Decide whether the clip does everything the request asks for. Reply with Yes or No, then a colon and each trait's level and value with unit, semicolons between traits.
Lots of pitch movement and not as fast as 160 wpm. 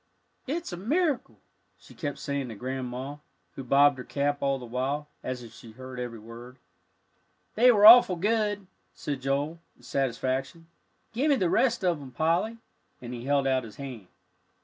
No: wide, 6.1 semitones; average, 170 wpm